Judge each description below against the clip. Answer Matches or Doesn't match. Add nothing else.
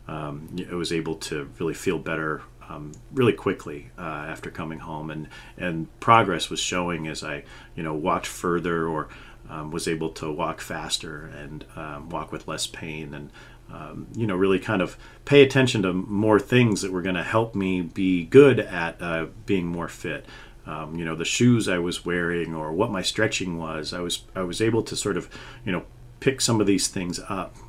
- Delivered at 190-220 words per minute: Matches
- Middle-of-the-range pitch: Doesn't match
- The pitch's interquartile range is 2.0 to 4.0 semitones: Doesn't match